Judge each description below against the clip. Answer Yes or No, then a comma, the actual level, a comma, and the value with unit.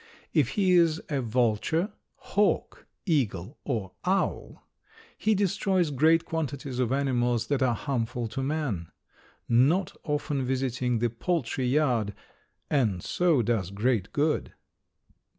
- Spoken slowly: Yes, slow, 120 wpm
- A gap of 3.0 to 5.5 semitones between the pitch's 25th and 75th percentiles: Yes, average, 5.0 semitones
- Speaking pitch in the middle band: No, low, 130 Hz